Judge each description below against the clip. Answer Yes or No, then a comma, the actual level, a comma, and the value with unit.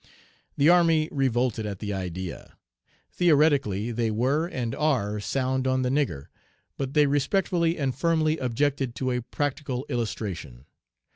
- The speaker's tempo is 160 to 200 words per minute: No, slow, 135 wpm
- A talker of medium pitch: No, low, 130 Hz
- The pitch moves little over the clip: No, average, 4.7 semitones